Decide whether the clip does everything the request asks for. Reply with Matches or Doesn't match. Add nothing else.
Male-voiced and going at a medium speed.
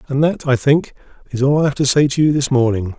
Doesn't match